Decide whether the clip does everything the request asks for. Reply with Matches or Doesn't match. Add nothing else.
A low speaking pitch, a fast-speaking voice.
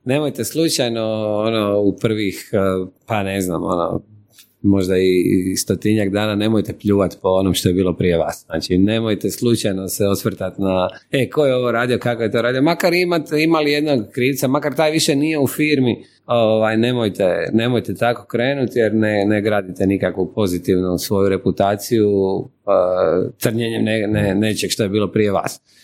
Matches